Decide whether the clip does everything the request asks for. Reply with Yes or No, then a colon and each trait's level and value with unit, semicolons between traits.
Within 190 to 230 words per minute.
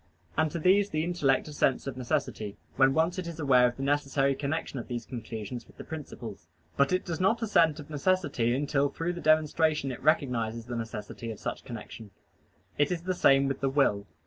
Yes: average, 200 wpm